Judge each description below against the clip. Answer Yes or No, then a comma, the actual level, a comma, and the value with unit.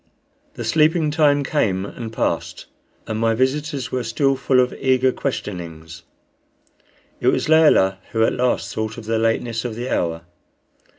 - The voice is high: No, low, 120 Hz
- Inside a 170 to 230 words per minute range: No, average, 155 wpm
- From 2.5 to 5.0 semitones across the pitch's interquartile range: Yes, average, 3.9 semitones